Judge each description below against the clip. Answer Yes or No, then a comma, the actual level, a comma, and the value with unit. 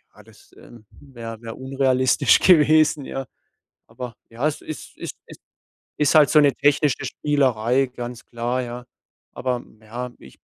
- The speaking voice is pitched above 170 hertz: No, low, 130 Hz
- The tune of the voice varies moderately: Yes, average, 3.1 semitones